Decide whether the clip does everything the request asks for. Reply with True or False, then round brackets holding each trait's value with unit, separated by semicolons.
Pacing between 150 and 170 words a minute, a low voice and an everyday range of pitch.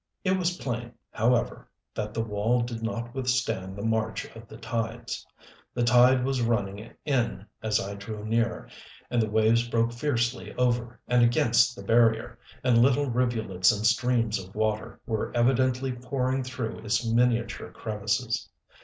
False (155 wpm; 115 Hz; 2.1 semitones)